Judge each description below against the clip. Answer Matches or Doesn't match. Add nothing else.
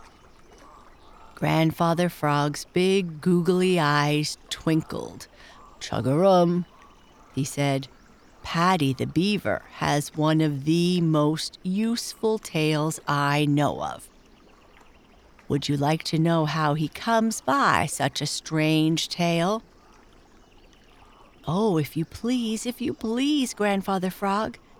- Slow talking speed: Matches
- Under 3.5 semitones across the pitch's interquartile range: Doesn't match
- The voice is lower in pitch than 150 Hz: Doesn't match